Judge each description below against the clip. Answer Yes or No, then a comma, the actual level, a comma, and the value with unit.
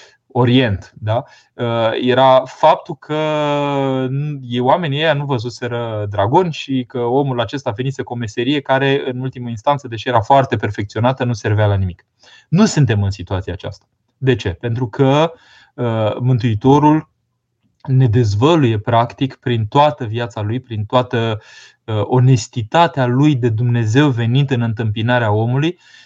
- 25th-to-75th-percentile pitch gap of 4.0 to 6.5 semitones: No, average, 3.0 semitones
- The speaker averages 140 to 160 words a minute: No, average, 130 wpm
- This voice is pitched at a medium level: No, low, 125 Hz